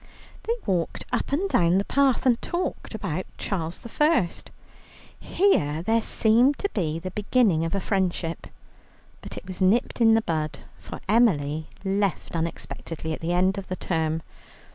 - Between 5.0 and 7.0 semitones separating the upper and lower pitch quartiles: Yes, wide, 5.6 semitones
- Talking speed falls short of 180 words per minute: Yes, average, 150 wpm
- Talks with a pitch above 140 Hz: Yes, high, 190 Hz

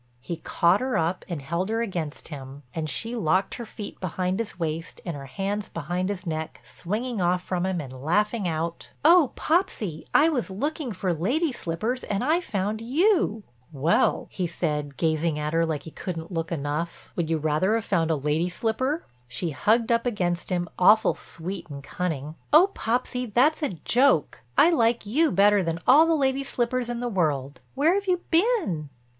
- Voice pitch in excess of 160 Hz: Yes, medium, 185 Hz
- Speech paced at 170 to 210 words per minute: Yes, average, 185 wpm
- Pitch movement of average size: No, wide, 6.8 semitones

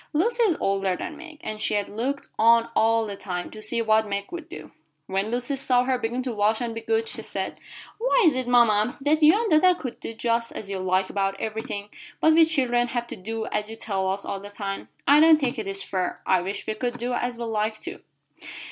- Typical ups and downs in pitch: Yes, average, 4.9 semitones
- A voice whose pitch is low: No, high, 230 Hz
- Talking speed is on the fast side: Yes, fast, 240 wpm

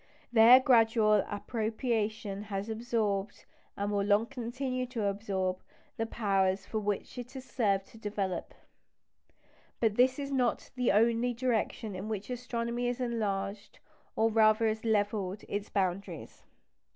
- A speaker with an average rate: No, slow, 130 wpm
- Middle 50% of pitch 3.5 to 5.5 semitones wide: No, average, 2.8 semitones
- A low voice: No, high, 220 Hz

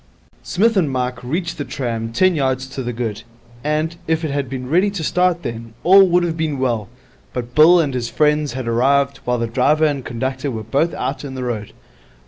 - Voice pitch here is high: No, low, 135 Hz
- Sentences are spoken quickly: Yes, fast, 210 wpm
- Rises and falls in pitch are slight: No, average, 4.6 semitones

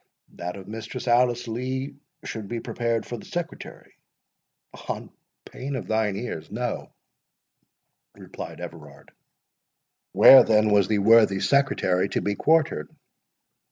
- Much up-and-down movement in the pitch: No, average, 3.7 semitones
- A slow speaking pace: Yes, slow, 120 wpm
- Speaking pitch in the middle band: No, low, 110 Hz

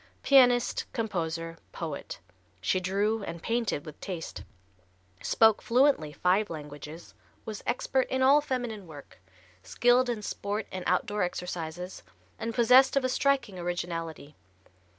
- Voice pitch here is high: Yes, high, 200 Hz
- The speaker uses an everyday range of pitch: No, wide, 6.5 semitones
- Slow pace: Yes, slow, 125 wpm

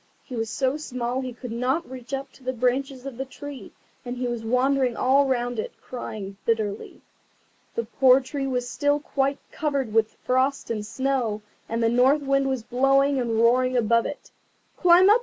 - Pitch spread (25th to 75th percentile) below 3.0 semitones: Yes, narrow, 2.5 semitones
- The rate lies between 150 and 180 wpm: No, average, 190 wpm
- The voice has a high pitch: Yes, very high, 255 Hz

